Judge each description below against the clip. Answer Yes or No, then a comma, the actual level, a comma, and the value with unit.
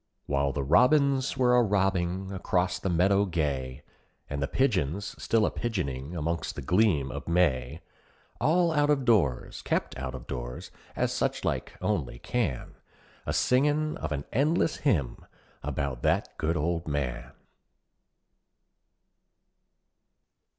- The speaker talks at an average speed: No, slow, 130 wpm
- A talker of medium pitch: No, very low, 90 Hz